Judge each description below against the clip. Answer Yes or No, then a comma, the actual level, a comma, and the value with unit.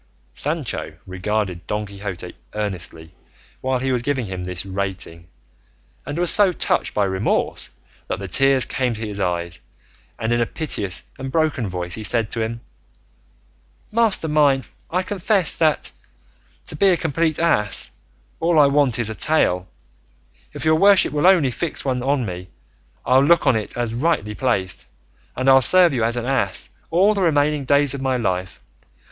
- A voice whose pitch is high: No, low, 125 Hz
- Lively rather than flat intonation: Yes, wide, 7.3 semitones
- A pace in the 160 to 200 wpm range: Yes, average, 170 wpm